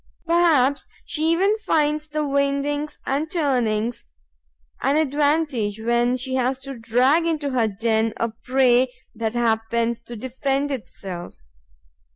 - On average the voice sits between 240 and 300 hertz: Yes, very high, 260 Hz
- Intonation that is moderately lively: Yes, average, 4.1 semitones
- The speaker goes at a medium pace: No, slow, 125 wpm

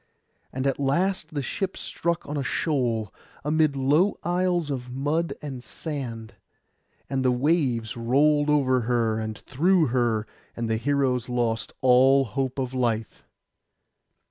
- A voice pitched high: No, low, 135 Hz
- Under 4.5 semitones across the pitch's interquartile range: Yes, average, 3.7 semitones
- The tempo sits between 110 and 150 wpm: Yes, average, 140 wpm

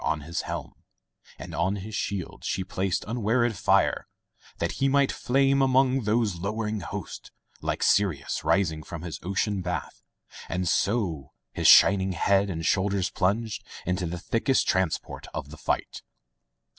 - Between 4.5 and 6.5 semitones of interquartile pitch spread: No, average, 4.1 semitones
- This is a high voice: No, very low, 95 Hz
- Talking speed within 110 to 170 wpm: Yes, average, 145 wpm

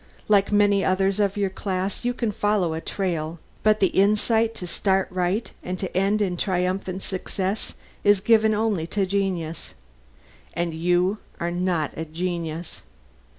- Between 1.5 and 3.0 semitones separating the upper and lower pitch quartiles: Yes, narrow, 2.6 semitones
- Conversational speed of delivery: Yes, average, 155 wpm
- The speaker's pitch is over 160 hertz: Yes, high, 190 Hz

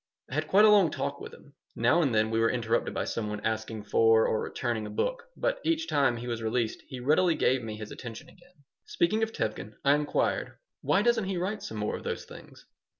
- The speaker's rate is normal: No, fast, 230 wpm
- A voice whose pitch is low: Yes, low, 125 Hz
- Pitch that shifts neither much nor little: No, wide, 8.2 semitones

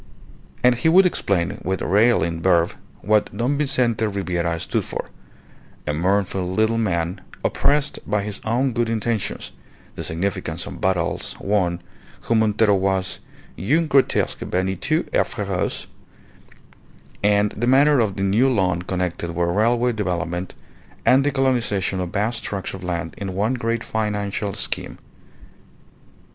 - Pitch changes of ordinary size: Yes, average, 4.2 semitones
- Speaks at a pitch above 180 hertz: No, low, 100 Hz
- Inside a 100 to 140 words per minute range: Yes, slow, 135 wpm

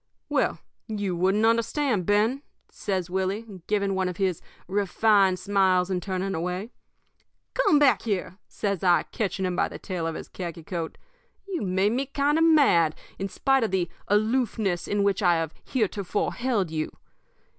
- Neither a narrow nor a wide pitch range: Yes, average, 3.3 semitones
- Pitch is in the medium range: No, high, 195 Hz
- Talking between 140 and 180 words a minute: Yes, average, 165 wpm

